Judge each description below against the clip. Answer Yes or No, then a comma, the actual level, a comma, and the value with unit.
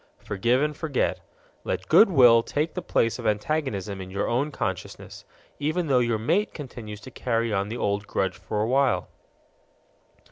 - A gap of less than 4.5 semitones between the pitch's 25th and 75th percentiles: No, wide, 5.5 semitones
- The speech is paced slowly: No, average, 170 wpm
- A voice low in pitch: Yes, low, 120 Hz